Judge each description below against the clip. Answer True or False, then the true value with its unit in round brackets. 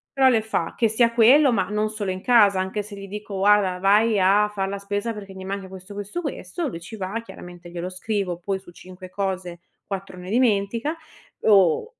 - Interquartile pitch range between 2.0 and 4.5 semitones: True (2.7 semitones)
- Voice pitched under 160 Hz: False (200 Hz)